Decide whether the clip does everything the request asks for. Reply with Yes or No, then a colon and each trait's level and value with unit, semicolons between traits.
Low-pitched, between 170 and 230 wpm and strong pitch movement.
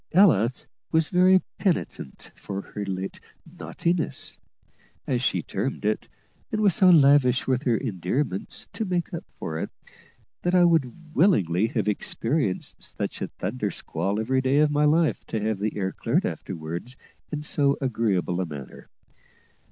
No: low, 130 Hz; average, 155 wpm; wide, 8.4 semitones